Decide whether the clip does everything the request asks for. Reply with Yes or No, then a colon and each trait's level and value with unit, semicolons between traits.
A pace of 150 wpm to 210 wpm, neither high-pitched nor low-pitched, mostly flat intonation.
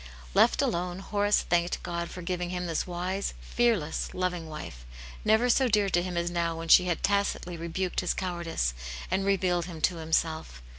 Yes: average, 180 wpm; medium, 175 Hz; narrow, 2.0 semitones